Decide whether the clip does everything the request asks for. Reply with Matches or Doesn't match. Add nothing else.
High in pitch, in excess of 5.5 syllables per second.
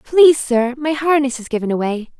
Doesn't match